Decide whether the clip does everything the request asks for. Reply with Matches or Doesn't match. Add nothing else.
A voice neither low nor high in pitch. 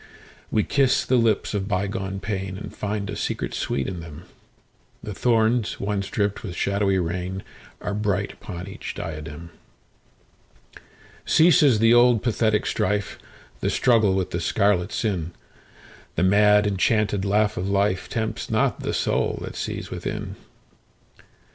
Doesn't match